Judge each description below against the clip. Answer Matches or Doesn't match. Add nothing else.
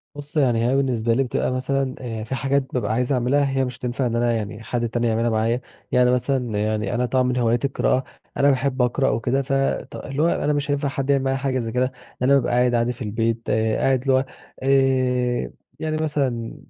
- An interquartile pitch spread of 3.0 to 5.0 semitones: Doesn't match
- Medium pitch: Doesn't match